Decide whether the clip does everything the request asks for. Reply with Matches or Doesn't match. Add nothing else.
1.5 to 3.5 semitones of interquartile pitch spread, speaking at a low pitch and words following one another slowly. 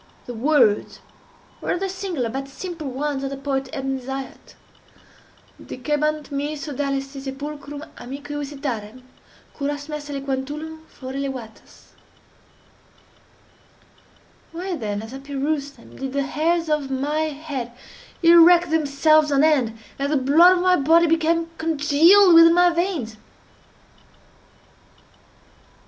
Doesn't match